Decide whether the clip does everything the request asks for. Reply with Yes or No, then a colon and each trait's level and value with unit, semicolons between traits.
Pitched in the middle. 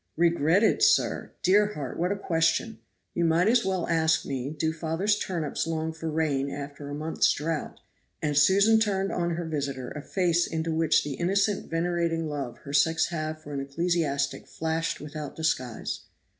Yes: medium, 160 Hz